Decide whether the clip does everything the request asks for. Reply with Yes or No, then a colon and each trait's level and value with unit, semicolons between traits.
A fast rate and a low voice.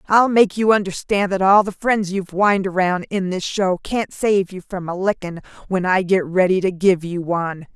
No: fast, 215 wpm; high, 190 Hz